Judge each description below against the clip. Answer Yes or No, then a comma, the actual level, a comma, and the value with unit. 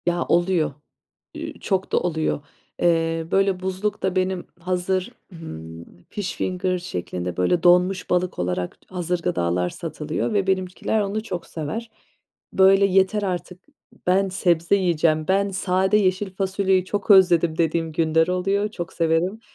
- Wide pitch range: No, average, 2.7 semitones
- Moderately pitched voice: Yes, medium, 180 Hz